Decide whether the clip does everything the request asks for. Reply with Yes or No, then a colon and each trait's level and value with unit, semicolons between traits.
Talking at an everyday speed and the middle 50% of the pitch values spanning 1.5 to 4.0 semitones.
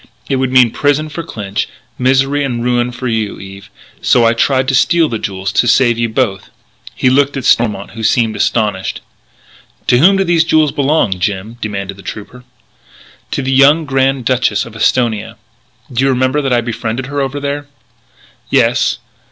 Yes: average, 175 wpm; average, 3.7 semitones